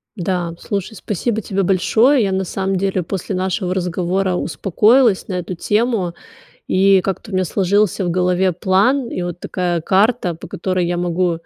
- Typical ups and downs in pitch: No, narrow, 2.1 semitones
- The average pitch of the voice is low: No, high, 190 Hz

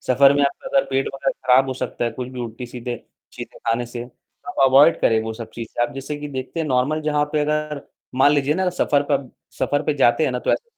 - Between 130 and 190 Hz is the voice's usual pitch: Yes, low, 135 Hz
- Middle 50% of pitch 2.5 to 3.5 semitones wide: Yes, average, 3.1 semitones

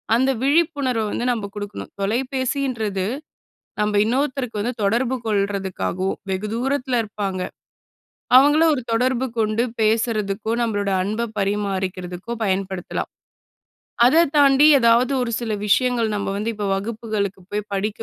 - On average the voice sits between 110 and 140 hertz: No, high, 220 Hz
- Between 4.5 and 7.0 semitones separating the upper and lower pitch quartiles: No, average, 4.0 semitones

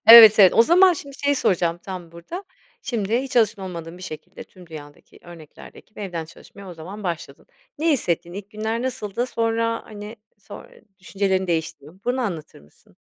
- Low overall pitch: No, high, 195 Hz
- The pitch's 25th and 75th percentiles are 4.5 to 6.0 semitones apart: Yes, average, 5.1 semitones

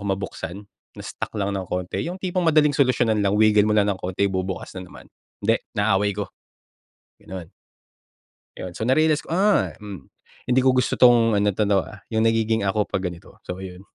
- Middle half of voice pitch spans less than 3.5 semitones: No, average, 4.1 semitones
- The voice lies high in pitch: No, low, 105 Hz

